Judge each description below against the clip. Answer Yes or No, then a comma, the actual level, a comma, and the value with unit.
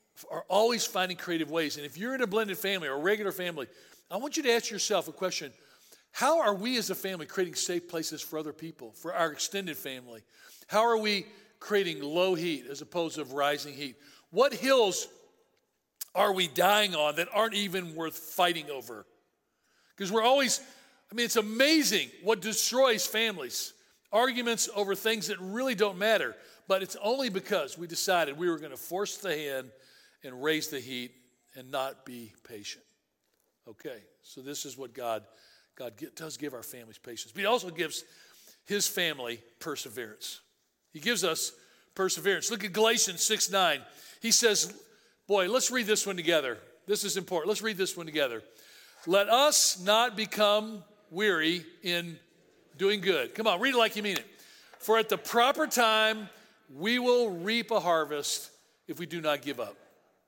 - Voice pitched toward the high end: Yes, high, 195 Hz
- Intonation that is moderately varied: No, wide, 5.7 semitones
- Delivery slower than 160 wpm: No, average, 175 wpm